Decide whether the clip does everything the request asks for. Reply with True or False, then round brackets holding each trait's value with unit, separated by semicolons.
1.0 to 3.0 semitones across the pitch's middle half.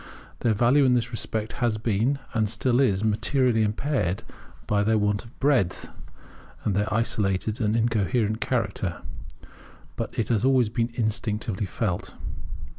True (2.6 semitones)